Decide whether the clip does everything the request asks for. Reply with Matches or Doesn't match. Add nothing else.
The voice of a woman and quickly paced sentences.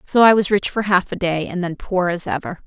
Matches